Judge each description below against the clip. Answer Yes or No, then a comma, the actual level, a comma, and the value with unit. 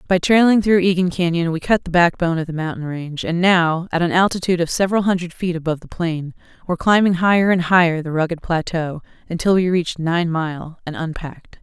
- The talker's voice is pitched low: No, medium, 170 Hz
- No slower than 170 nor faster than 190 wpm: No, fast, 205 wpm